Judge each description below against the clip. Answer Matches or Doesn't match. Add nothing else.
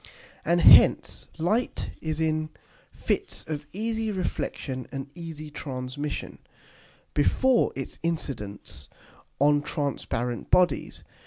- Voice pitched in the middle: Matches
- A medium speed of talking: Doesn't match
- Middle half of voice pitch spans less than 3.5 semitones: Doesn't match